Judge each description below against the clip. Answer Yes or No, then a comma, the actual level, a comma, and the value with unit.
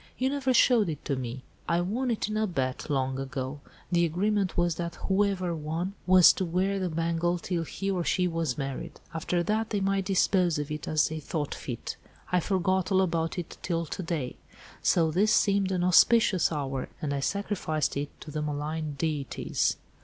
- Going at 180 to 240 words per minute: Yes, average, 190 wpm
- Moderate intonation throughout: Yes, average, 4.0 semitones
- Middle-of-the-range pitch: Yes, medium, 170 Hz